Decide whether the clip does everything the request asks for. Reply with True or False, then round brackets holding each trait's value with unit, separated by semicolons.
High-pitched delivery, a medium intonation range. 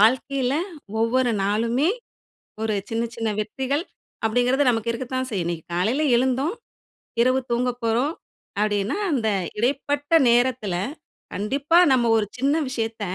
True (245 Hz; 3.0 semitones)